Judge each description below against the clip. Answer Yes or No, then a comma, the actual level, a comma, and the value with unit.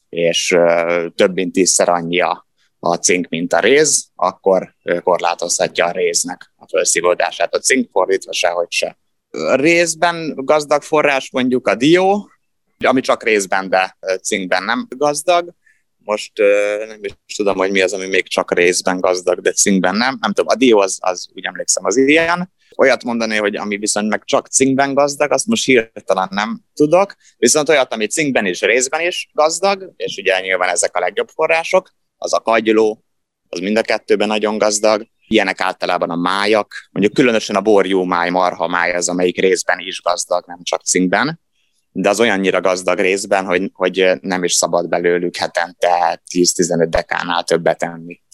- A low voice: Yes, low, 105 Hz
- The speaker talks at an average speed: No, fast, 165 wpm